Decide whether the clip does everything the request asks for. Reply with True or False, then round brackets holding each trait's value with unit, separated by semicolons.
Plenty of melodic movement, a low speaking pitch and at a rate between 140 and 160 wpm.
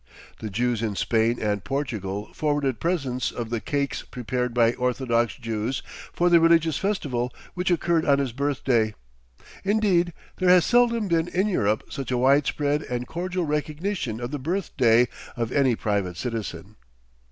True (6.2 semitones; 130 Hz; 150 wpm)